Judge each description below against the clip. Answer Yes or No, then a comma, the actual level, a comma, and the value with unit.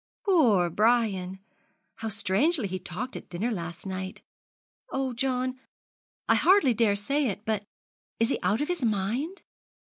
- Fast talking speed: No, average, 145 wpm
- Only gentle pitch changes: No, wide, 5.4 semitones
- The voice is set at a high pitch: Yes, high, 225 Hz